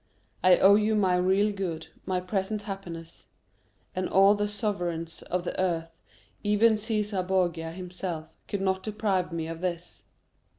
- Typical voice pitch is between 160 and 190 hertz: Yes, medium, 185 Hz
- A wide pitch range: No, average, 2.8 semitones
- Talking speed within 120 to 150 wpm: Yes, average, 145 wpm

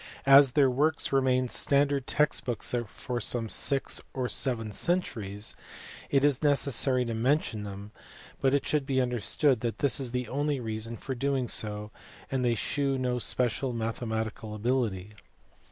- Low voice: Yes, low, 125 Hz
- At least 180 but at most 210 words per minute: No, average, 155 wpm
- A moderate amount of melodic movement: Yes, average, 3.6 semitones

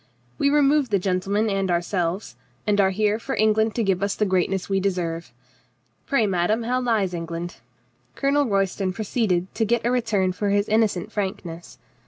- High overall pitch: Yes, high, 200 Hz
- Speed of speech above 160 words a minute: Yes, average, 180 wpm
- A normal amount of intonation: Yes, average, 3.3 semitones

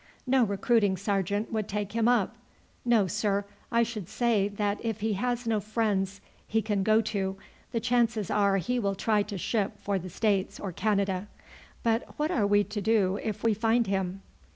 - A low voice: No, high, 210 Hz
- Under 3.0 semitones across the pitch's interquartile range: Yes, narrow, 2.4 semitones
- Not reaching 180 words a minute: No, average, 185 wpm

